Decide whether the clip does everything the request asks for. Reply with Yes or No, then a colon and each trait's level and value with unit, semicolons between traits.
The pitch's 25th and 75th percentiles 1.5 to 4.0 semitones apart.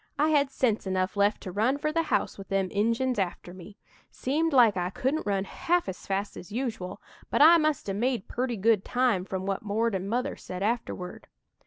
No: average, 5.2 semitones